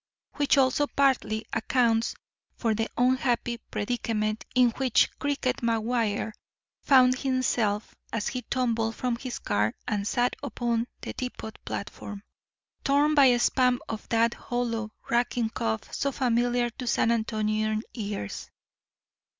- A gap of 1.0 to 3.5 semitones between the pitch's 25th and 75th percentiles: Yes, narrow, 2.4 semitones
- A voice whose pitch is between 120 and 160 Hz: No, high, 235 Hz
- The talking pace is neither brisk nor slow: No, slow, 125 wpm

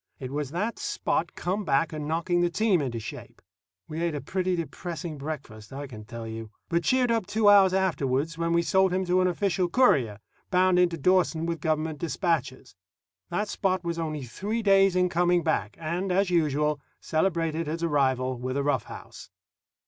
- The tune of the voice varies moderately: Yes, average, 4.1 semitones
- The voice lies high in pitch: No, medium, 170 Hz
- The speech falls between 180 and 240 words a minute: Yes, average, 185 wpm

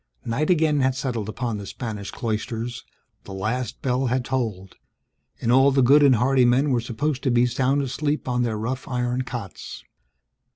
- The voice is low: Yes, low, 125 Hz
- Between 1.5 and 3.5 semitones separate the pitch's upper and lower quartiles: Yes, narrow, 2.5 semitones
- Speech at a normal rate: Yes, average, 180 wpm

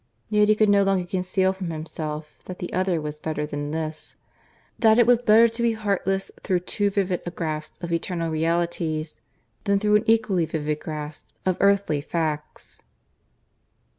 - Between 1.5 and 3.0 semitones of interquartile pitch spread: No, average, 4.3 semitones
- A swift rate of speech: No, average, 165 wpm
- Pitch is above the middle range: No, medium, 180 Hz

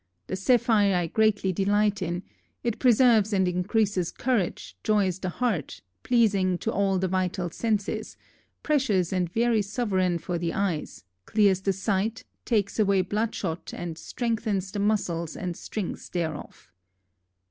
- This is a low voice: No, high, 195 Hz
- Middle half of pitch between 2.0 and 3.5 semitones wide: Yes, average, 3.2 semitones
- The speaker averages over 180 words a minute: No, slow, 135 wpm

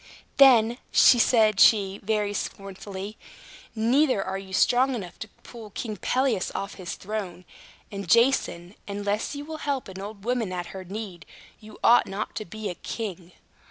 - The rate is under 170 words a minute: Yes, average, 160 wpm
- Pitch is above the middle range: Yes, high, 210 Hz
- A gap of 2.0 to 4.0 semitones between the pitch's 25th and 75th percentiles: Yes, average, 3.3 semitones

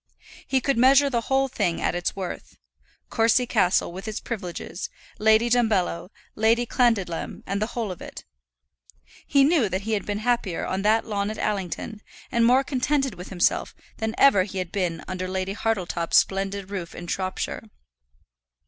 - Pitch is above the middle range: Yes, high, 210 Hz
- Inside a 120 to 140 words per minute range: No, average, 170 wpm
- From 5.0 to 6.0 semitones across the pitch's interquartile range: No, average, 4.2 semitones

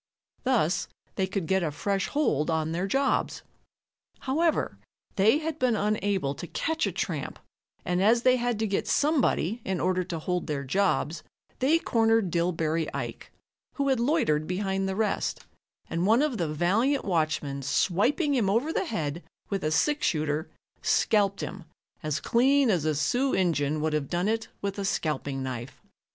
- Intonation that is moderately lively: No, wide, 7.0 semitones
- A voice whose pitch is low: No, high, 195 Hz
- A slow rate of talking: No, average, 170 wpm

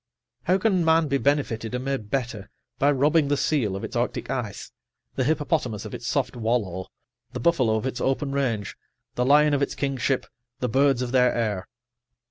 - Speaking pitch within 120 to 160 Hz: Yes, low, 135 Hz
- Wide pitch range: No, average, 3.8 semitones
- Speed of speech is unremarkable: Yes, average, 185 wpm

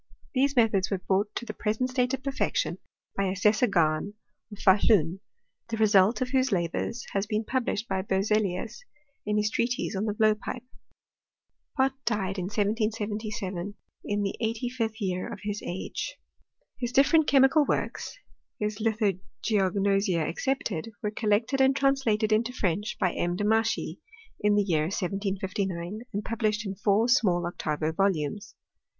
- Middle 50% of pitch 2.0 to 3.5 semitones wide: Yes, average, 3.1 semitones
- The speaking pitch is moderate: No, high, 210 Hz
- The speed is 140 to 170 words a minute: Yes, average, 150 wpm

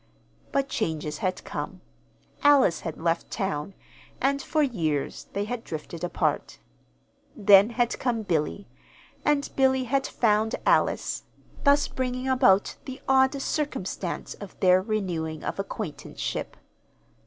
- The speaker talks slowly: Yes, slow, 120 wpm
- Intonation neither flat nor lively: No, wide, 6.6 semitones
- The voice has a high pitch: Yes, high, 215 Hz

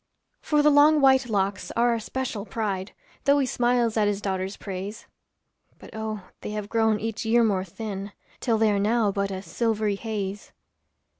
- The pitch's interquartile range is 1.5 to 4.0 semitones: Yes, average, 2.9 semitones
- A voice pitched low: No, high, 215 Hz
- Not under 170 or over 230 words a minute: Yes, average, 175 wpm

